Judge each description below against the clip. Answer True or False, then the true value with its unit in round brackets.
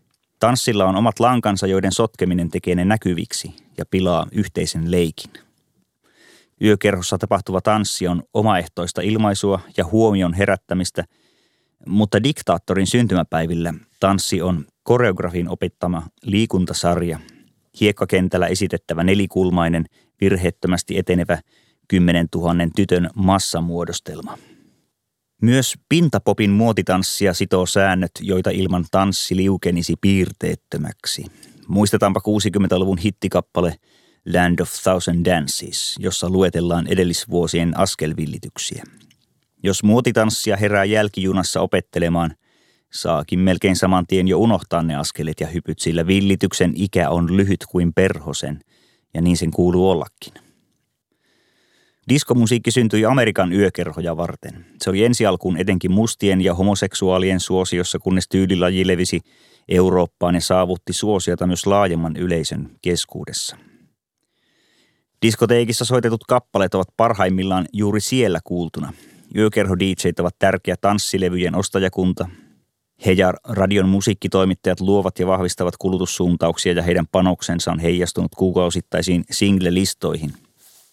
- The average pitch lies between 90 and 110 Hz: True (95 Hz)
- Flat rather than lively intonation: True (2.3 semitones)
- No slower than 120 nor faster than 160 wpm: False (105 wpm)